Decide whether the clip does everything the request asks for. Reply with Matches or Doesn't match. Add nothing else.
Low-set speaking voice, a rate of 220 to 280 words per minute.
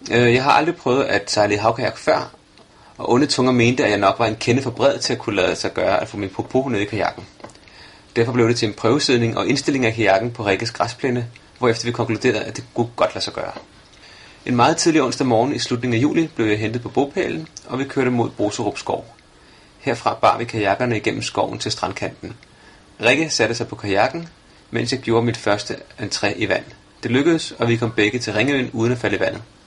Matches